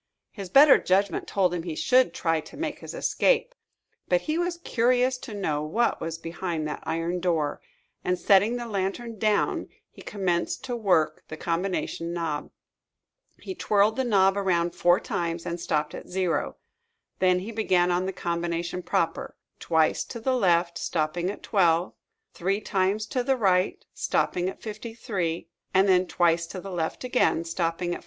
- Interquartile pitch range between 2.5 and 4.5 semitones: Yes, average, 4.2 semitones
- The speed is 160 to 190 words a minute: Yes, average, 170 wpm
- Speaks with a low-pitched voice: No, medium, 185 Hz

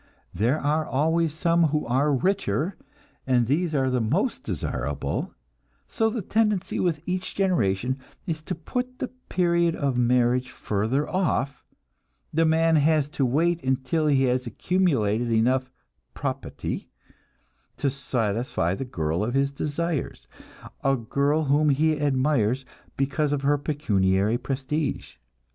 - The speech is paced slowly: Yes, slow, 130 wpm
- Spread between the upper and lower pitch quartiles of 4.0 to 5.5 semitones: Yes, average, 4.4 semitones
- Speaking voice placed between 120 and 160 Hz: Yes, medium, 140 Hz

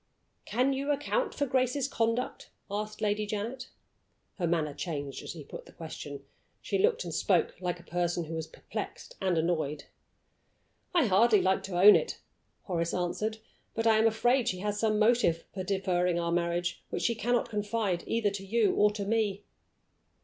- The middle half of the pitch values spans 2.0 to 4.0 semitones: No, average, 4.8 semitones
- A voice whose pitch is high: Yes, high, 205 Hz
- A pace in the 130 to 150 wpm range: No, average, 175 wpm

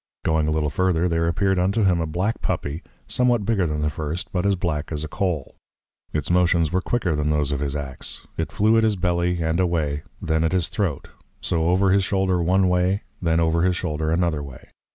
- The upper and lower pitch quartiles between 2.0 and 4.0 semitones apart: Yes, average, 3.2 semitones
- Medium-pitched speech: No, very low, 85 Hz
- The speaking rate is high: Yes, fast, 220 wpm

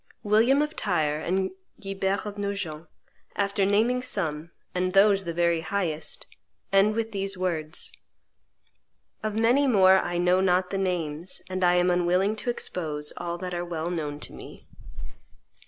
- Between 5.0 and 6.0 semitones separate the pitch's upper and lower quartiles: No, average, 2.8 semitones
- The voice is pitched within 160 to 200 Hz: Yes, medium, 185 Hz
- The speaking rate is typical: Yes, average, 155 wpm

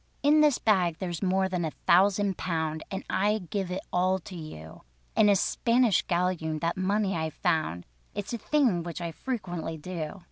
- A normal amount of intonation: Yes, average, 3.5 semitones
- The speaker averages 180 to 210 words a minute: Yes, average, 185 wpm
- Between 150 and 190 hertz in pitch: Yes, medium, 185 Hz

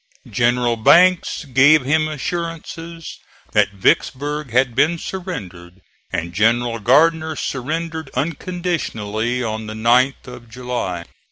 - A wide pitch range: Yes, wide, 5.7 semitones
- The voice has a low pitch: Yes, low, 130 Hz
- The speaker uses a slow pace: Yes, slow, 105 wpm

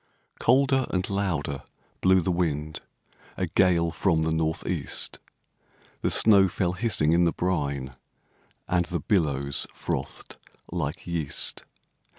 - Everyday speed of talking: No, slow, 125 wpm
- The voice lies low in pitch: Yes, very low, 85 Hz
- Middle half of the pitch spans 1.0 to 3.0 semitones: No, average, 3.4 semitones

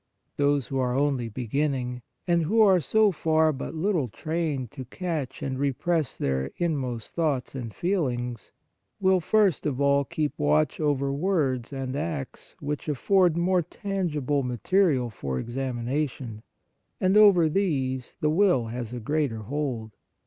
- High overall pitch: No, medium, 140 Hz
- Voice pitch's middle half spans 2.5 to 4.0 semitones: No, average, 5.1 semitones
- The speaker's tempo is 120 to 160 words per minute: Yes, average, 140 wpm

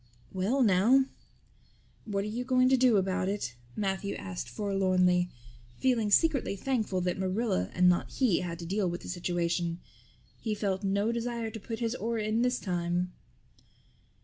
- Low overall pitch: No, high, 200 Hz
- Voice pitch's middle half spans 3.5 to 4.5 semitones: Yes, average, 4.2 semitones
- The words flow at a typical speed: Yes, average, 160 wpm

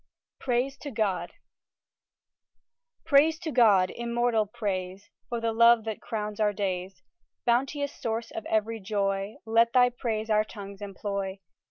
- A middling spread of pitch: Yes, average, 3.0 semitones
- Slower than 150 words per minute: Yes, slow, 135 wpm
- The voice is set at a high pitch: Yes, high, 220 Hz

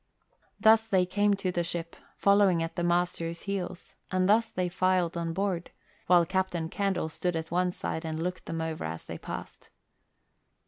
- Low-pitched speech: No, medium, 180 Hz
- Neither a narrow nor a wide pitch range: No, narrow, 2.3 semitones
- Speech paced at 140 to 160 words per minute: No, average, 175 wpm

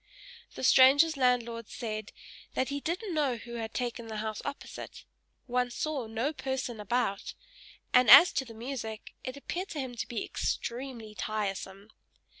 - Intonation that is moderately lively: Yes, average, 3.5 semitones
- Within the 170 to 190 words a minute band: No, average, 155 wpm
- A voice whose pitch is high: Yes, high, 245 Hz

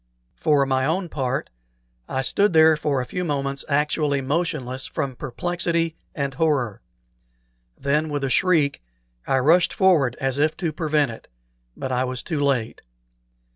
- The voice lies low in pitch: No, medium, 145 Hz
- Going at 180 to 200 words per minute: No, average, 145 wpm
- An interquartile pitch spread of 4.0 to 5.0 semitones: No, average, 3.3 semitones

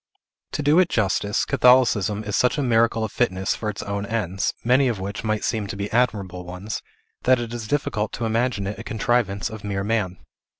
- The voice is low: Yes, low, 110 Hz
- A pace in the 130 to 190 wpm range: No, fast, 205 wpm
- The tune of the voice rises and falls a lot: No, average, 3.2 semitones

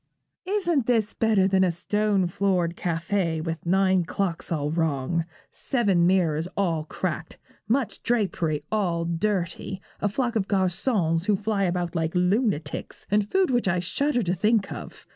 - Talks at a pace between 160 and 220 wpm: No, average, 150 wpm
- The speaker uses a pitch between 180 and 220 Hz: Yes, medium, 185 Hz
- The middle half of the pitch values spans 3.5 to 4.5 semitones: Yes, average, 3.9 semitones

